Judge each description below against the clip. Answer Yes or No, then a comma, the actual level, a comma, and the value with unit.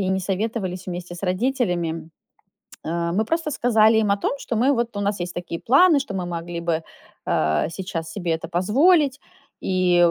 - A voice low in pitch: No, high, 190 Hz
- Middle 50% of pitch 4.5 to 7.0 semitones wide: Yes, average, 5.0 semitones